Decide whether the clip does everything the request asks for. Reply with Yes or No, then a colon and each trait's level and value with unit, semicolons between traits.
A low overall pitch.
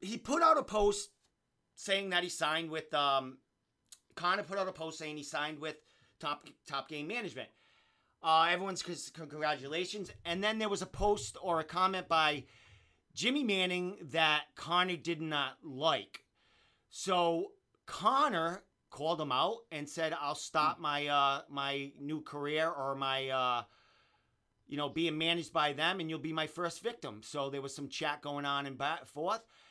No: medium, 160 Hz